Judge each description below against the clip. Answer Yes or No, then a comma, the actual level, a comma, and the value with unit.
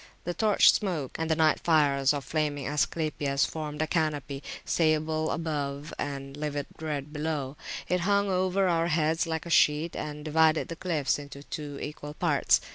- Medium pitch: Yes, medium, 155 Hz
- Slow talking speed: No, average, 170 wpm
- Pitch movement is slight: Yes, narrow, 2.0 semitones